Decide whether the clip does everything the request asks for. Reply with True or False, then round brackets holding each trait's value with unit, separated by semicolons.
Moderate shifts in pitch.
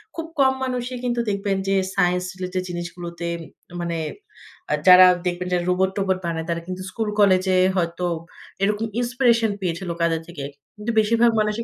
True (3.9 semitones)